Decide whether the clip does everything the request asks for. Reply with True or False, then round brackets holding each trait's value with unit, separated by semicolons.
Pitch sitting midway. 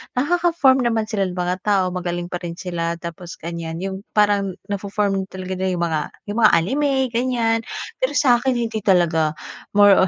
False (195 Hz)